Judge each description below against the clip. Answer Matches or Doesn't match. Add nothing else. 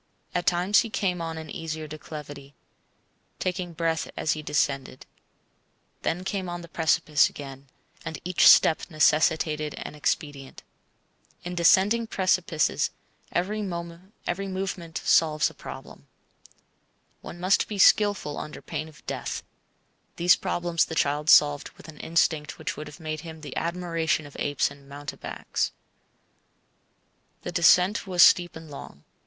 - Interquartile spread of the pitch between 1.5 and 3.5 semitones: Matches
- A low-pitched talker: Doesn't match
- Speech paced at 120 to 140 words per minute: Matches